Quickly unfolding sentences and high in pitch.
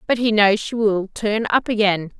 Yes: fast, 220 wpm; high, 210 Hz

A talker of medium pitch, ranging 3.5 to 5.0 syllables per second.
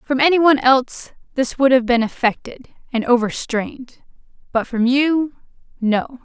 No: very high, 255 Hz; 4.8 syllables/s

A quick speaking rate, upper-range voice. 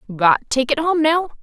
Yes: fast, 210 wpm; very high, 280 Hz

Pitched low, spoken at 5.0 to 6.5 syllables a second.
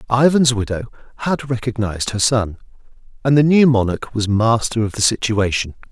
Yes: low, 115 Hz; 5.4 syllables/s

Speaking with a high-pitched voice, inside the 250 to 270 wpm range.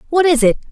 Yes: very high, 300 Hz; fast, 255 wpm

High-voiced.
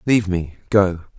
No: very low, 95 Hz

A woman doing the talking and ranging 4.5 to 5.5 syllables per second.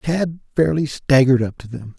No: male; 5.3 syllables/s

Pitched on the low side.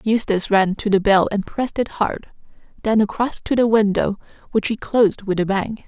No: high, 210 Hz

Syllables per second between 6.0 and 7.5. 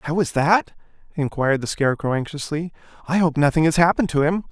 Yes: 6.5 syllables/s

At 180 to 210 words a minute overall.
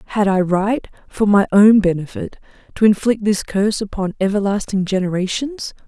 No: average, 145 wpm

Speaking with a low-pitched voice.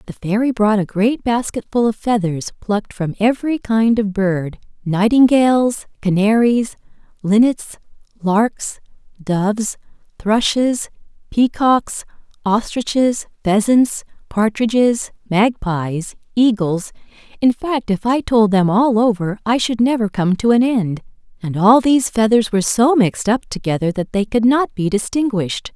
No: high, 220 Hz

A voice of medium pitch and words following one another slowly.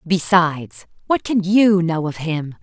No: medium, 175 Hz; average, 160 wpm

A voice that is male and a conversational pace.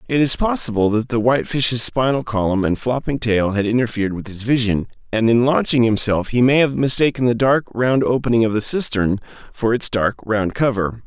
Yes: male; average, 195 wpm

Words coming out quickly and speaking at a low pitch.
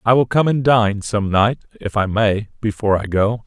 Yes: fast, 225 wpm; low, 110 Hz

